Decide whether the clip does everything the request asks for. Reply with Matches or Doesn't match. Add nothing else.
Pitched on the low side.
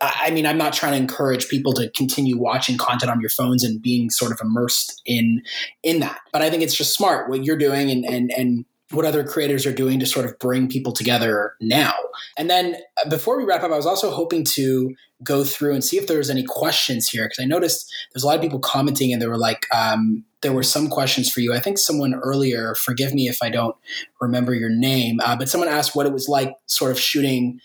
Matches